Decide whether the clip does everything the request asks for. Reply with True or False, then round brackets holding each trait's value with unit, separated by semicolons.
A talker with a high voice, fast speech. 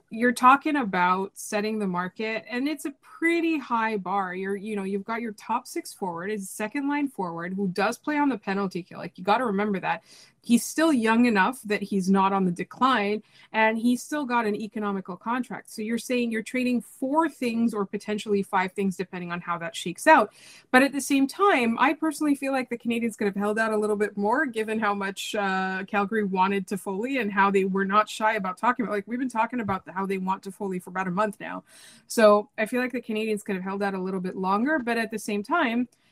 True (215 Hz; 240 wpm)